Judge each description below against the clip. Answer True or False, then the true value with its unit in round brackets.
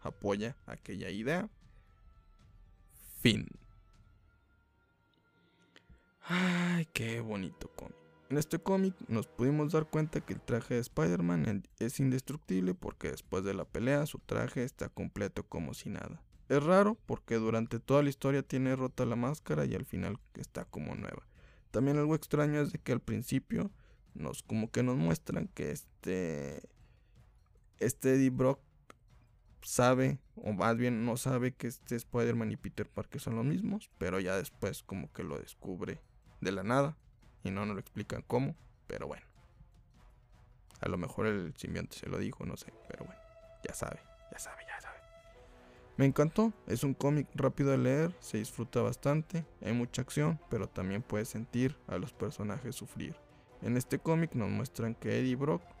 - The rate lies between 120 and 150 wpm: False (160 wpm)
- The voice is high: False (125 Hz)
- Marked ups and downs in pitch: False (4.7 semitones)